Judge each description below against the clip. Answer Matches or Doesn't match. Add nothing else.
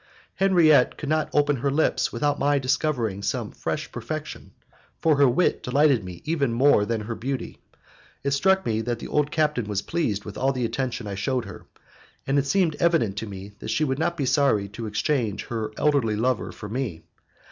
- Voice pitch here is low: Matches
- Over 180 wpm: Matches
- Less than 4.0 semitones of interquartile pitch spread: Doesn't match